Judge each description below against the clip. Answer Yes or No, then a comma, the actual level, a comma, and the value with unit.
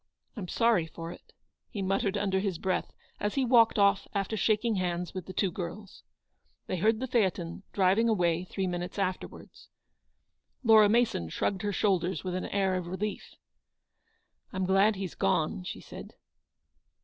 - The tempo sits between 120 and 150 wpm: No, average, 165 wpm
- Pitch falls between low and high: No, high, 195 Hz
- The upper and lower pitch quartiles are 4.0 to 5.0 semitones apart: No, average, 2.7 semitones